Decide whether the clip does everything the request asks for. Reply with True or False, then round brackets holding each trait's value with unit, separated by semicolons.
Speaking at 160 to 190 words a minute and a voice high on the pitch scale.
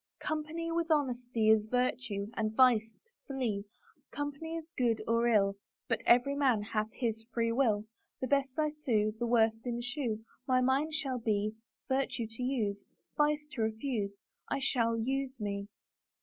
True (165 wpm; 240 Hz)